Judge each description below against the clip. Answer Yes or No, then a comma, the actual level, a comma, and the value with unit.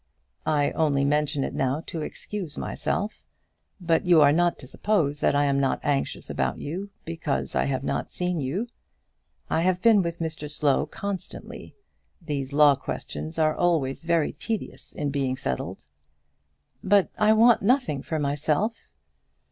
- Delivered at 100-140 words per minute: No, average, 155 wpm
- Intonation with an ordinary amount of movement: Yes, average, 4.2 semitones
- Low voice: No, medium, 155 Hz